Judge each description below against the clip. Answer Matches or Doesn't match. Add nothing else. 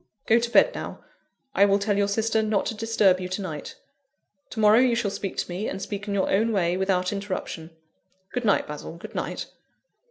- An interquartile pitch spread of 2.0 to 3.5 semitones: Matches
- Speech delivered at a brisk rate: Matches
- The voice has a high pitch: Matches